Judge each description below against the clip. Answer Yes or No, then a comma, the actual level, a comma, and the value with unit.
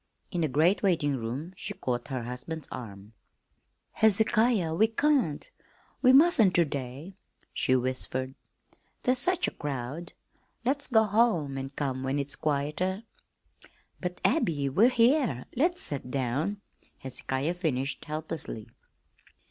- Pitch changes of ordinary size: No, wide, 8.2 semitones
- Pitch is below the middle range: No, medium, 155 Hz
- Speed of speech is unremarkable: No, slow, 125 wpm